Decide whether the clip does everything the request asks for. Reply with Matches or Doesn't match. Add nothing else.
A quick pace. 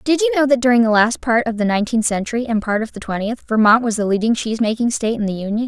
Matches